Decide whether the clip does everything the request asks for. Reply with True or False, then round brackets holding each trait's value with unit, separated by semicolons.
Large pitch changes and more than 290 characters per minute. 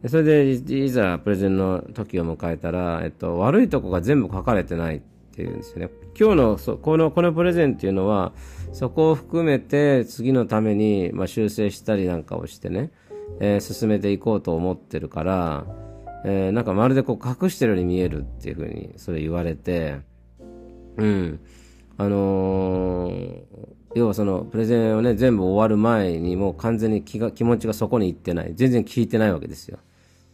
False (5.0 semitones; 350 characters per minute)